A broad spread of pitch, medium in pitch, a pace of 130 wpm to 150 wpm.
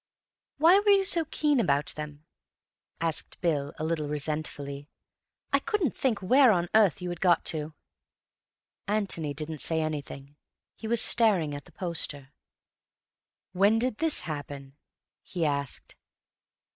Yes: wide, 7.1 semitones; medium, 165 Hz; slow, 135 wpm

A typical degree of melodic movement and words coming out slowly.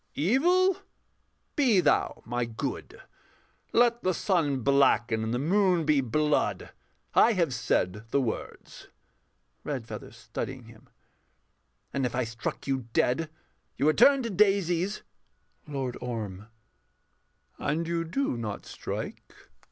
No: wide, 7.8 semitones; slow, 120 wpm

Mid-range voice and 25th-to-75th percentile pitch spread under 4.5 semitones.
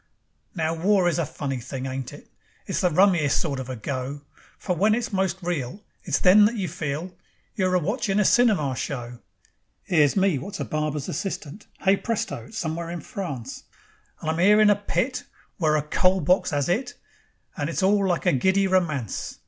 No: medium, 175 Hz; average, 5.3 semitones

